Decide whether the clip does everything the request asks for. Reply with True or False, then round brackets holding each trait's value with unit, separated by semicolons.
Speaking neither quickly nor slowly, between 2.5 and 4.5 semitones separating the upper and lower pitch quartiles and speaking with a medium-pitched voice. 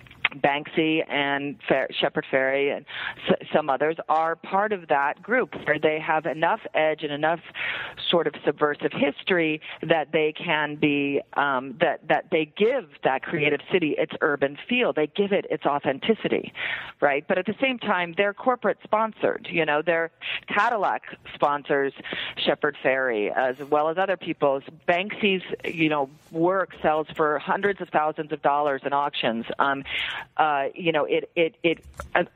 True (160 wpm; 3.7 semitones; 155 Hz)